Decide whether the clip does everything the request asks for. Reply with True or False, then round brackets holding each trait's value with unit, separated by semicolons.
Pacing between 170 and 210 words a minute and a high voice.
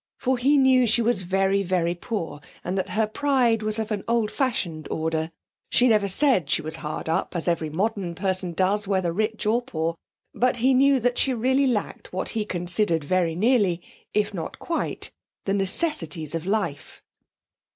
True (180 wpm; 200 Hz)